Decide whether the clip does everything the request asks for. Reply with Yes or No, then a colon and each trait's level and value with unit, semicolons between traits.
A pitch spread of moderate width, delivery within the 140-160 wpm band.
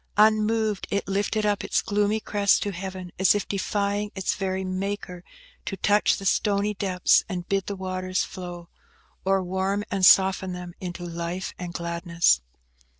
No: narrow, 2.0 semitones; average, 155 wpm